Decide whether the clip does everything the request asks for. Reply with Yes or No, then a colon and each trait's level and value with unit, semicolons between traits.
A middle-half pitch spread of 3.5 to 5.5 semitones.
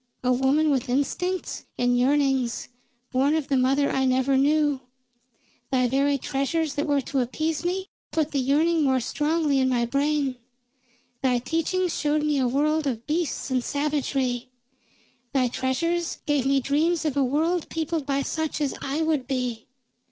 No: average, 3.0 semitones